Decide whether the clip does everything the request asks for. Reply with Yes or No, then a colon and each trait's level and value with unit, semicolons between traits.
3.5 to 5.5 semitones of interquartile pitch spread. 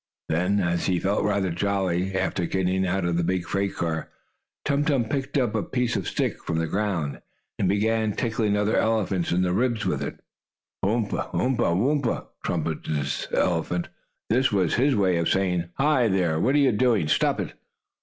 Yes: average, 4.6 semitones